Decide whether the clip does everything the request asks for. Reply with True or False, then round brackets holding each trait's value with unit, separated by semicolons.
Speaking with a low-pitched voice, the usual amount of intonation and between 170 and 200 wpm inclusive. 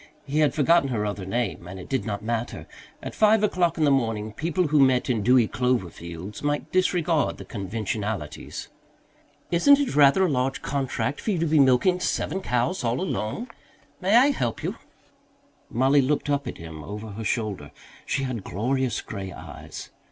False (130 Hz; 6.6 semitones; 180 wpm)